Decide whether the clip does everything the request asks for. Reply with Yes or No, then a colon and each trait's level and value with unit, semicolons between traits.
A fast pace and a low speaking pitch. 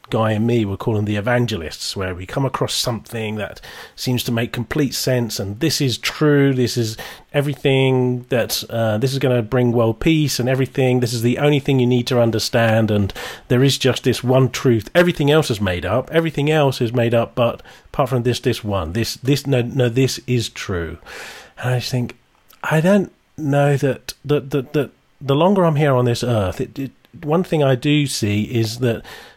Yes: fast, 215 wpm; low, 125 Hz